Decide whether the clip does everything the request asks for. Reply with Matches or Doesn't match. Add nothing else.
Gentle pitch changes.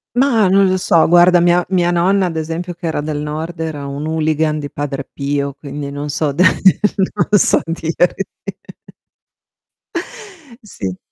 Doesn't match